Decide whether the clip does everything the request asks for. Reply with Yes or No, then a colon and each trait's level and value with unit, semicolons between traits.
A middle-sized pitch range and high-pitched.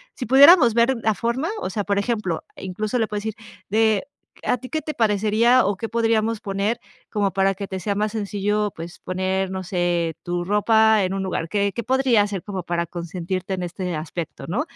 Yes: average, 3.2 semitones; high, 205 Hz